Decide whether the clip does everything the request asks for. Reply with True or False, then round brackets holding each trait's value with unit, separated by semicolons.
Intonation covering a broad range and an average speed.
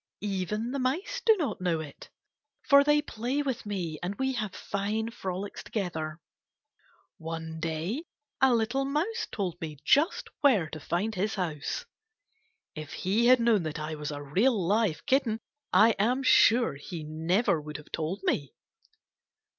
True (7.5 semitones; 155 wpm)